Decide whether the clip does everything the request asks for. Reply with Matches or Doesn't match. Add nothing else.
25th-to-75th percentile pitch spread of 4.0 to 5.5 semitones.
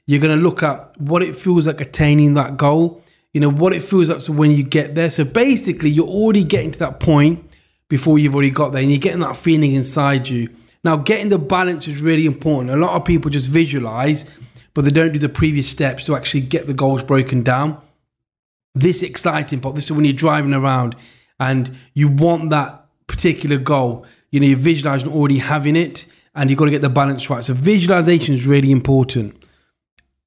Doesn't match